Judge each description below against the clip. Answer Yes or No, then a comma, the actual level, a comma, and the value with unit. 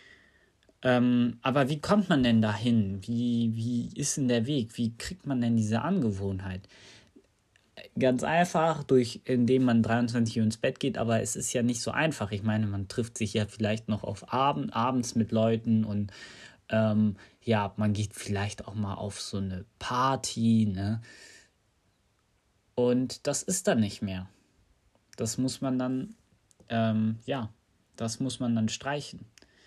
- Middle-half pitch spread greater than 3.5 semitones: No, average, 3.1 semitones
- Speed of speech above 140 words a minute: Yes, average, 160 wpm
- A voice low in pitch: Yes, low, 115 Hz